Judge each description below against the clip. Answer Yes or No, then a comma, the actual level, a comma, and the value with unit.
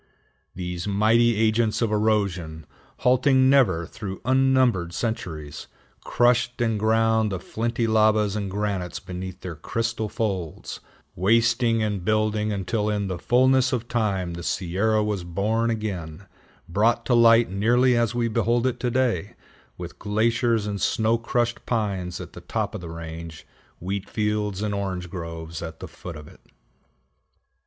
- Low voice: Yes, low, 105 Hz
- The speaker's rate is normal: Yes, average, 145 wpm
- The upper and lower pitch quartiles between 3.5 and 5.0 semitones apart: Yes, average, 4.0 semitones